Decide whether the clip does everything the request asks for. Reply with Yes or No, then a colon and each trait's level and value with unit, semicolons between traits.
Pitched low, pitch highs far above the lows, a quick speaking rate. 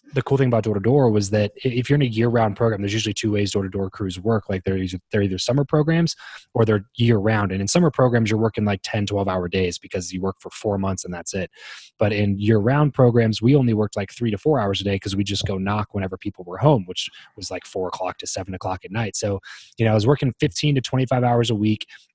No: low, 105 Hz; average, 3.6 semitones; fast, 255 wpm